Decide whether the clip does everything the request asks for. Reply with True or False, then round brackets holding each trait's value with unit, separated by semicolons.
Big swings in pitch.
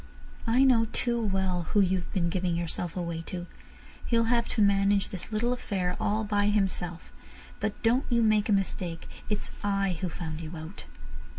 False (3.5 semitones)